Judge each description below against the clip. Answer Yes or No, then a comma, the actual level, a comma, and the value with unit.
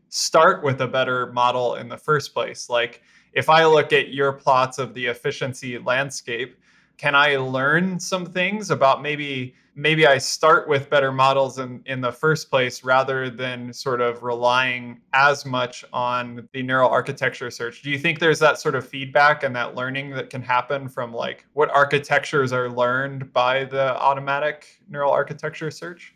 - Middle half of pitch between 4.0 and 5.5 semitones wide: No, narrow, 2.4 semitones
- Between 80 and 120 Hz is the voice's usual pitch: No, low, 135 Hz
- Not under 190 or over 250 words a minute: No, average, 175 wpm